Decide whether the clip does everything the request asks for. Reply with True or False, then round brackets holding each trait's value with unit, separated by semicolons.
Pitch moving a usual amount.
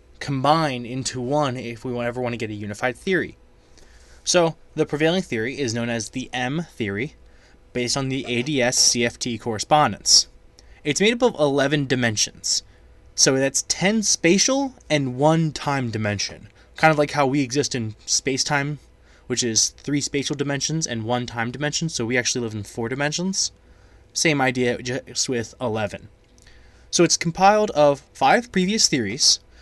True (4.4 semitones)